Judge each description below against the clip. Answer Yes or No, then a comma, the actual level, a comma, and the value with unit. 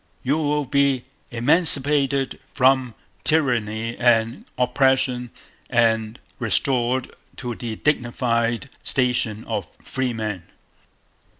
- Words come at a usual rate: No, slow, 85 wpm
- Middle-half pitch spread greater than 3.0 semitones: No, average, 2.7 semitones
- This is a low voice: Yes, low, 125 Hz